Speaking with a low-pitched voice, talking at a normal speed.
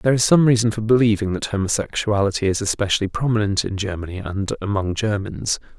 Yes: low, 105 Hz; average, 165 wpm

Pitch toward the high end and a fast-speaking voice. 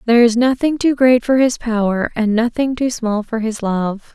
Yes: high, 235 Hz; fast, 215 wpm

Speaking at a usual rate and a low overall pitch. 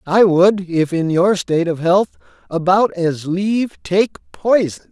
No: average, 160 wpm; medium, 175 Hz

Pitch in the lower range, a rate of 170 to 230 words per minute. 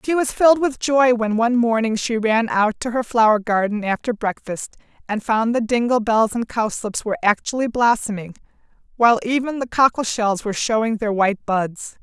No: high, 225 Hz; average, 185 wpm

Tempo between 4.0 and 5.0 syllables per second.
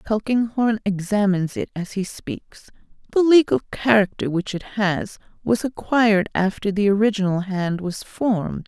Yes: 4.8 syllables/s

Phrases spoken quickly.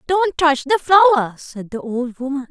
No: average, 190 wpm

